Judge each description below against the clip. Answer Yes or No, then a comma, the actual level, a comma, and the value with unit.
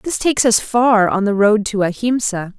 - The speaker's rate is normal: No, fast, 210 wpm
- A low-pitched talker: No, high, 215 Hz